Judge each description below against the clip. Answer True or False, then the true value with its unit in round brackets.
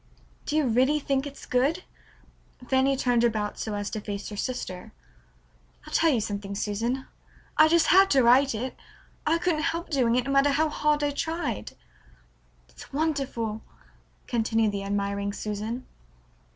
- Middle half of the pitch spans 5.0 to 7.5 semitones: True (5.5 semitones)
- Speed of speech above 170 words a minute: False (155 wpm)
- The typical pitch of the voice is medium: False (255 Hz)